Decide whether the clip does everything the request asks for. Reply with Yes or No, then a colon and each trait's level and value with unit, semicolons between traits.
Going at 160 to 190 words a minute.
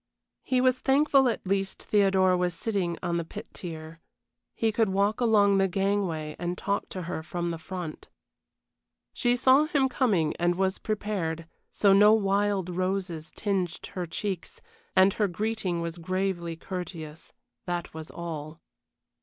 No: average, 150 wpm